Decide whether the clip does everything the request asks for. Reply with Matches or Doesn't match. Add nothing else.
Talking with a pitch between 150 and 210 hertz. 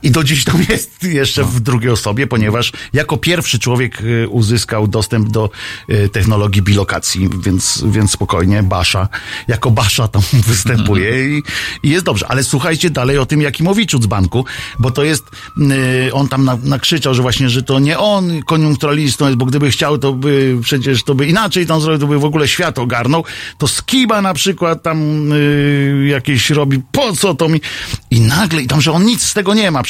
Doesn't match